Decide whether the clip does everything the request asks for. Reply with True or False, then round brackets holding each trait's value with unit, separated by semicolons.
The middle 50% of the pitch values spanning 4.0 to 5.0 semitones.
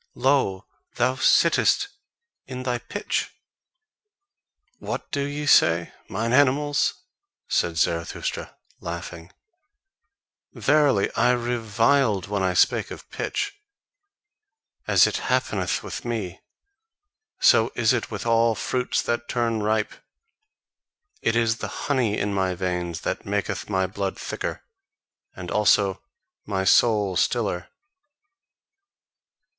True (4.7 semitones)